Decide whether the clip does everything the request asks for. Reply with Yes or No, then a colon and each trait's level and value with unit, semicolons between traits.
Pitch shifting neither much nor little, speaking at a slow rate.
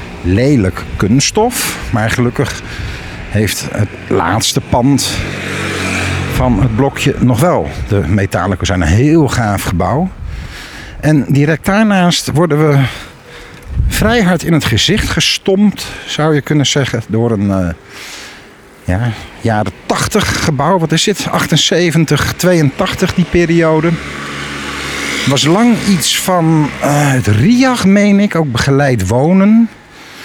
No: wide, 8.8 semitones; slow, 125 wpm